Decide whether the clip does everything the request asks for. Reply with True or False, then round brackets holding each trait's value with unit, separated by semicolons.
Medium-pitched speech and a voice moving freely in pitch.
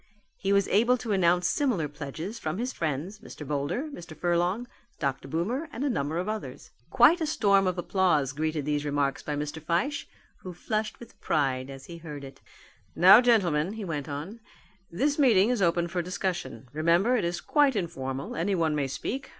True (175 Hz; 6.2 semitones)